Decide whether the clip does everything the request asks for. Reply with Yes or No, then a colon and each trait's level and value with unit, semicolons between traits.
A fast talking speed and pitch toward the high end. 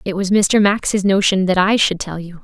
Yes: fast, 245 wpm; high, 195 Hz